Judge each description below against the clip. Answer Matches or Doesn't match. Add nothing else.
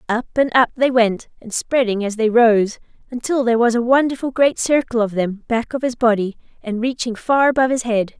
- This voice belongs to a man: Doesn't match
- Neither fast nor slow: Doesn't match